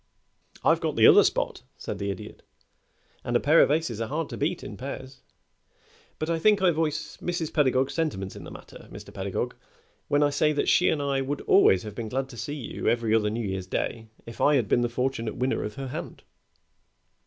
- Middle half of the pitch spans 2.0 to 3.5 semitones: No, average, 5.1 semitones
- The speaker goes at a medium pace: No, fast, 215 wpm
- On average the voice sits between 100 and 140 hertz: Yes, low, 135 Hz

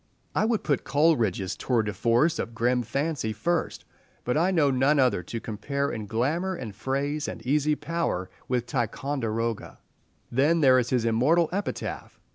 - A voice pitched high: No, low, 130 Hz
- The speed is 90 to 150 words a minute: No, average, 160 wpm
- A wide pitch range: No, average, 4.8 semitones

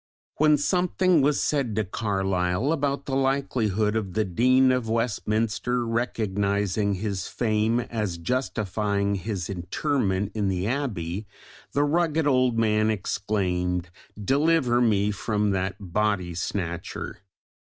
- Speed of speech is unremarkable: No, slow, 120 wpm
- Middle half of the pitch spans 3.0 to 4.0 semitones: No, average, 4.7 semitones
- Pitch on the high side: No, low, 110 Hz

